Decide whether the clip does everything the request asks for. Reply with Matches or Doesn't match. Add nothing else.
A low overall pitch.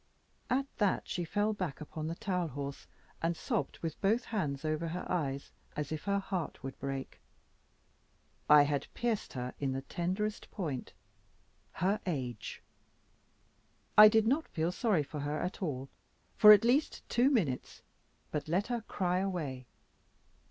Doesn't match